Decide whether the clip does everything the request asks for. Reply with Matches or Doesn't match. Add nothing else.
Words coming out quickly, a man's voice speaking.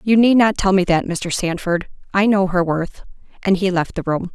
Doesn't match